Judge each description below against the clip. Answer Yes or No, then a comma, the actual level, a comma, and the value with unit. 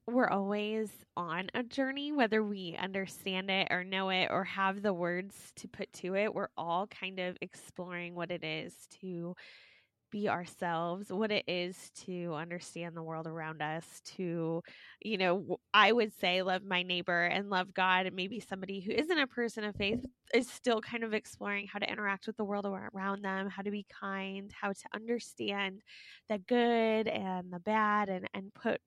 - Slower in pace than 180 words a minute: No, average, 185 wpm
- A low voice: No, high, 195 Hz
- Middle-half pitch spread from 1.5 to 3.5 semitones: Yes, average, 2.8 semitones